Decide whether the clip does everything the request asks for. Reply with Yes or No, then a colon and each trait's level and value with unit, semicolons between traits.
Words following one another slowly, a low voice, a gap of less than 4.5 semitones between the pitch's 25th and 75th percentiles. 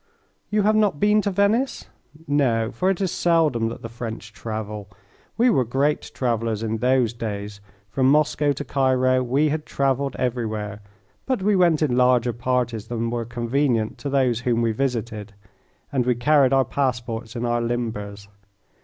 No: average, 165 wpm; low, 125 Hz; average, 4.0 semitones